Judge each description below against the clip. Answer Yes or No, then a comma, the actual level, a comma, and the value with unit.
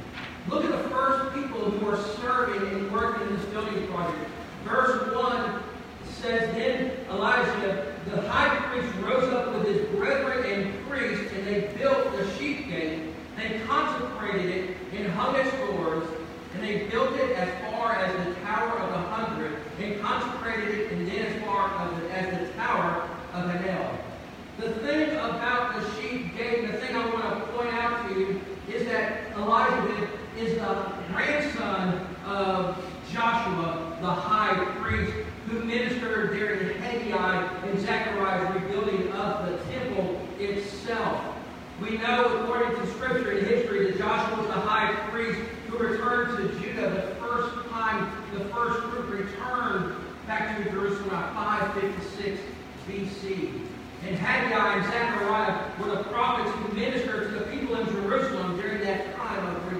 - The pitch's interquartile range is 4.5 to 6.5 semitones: No, average, 3.3 semitones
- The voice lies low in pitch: No, high, 210 Hz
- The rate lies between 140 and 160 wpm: Yes, average, 155 wpm